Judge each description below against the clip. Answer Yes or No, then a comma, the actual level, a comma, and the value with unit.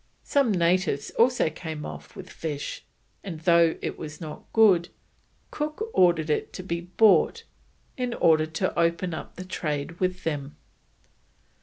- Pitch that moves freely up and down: No, average, 3.2 semitones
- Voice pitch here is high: No, medium, 170 Hz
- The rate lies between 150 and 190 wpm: No, average, 140 wpm